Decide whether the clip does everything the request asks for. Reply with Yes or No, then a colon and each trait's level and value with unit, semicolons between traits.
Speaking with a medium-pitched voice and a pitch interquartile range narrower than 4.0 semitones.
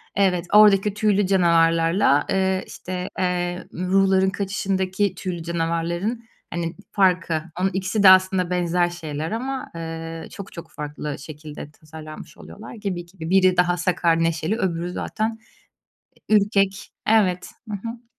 Yes: medium, 180 Hz; average, 2.9 semitones